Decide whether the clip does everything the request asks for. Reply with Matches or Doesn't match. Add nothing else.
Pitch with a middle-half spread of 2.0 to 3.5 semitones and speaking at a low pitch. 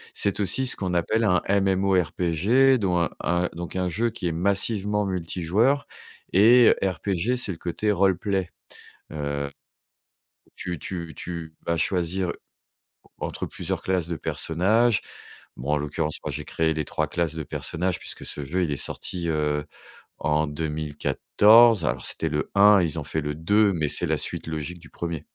Doesn't match